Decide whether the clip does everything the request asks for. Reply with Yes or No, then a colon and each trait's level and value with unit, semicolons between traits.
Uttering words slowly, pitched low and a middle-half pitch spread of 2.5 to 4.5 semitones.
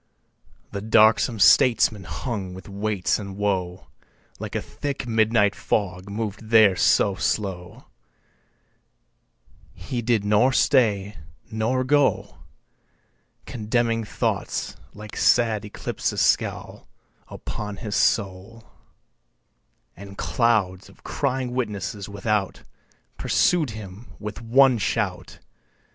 Yes: slow, 100 wpm; low, 105 Hz; average, 2.8 semitones